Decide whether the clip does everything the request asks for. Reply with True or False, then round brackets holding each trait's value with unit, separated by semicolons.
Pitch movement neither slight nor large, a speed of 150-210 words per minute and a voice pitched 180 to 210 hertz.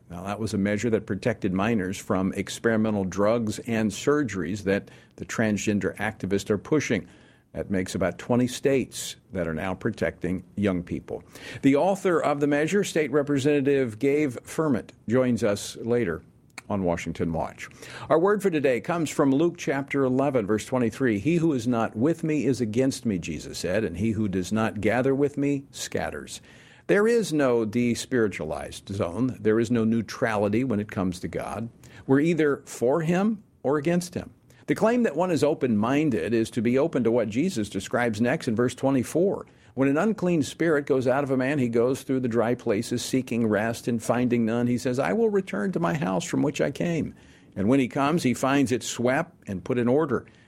False (5.0 semitones; 190 wpm; 120 Hz)